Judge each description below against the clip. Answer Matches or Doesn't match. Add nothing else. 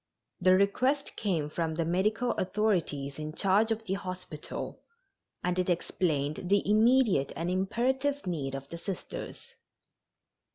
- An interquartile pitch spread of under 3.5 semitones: Doesn't match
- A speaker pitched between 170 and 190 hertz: Matches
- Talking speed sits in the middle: Doesn't match